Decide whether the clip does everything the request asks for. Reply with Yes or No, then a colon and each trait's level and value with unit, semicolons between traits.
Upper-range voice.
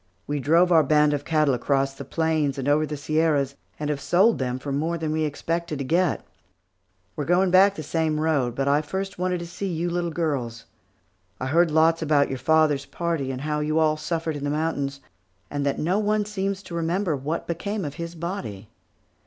No: medium, 155 Hz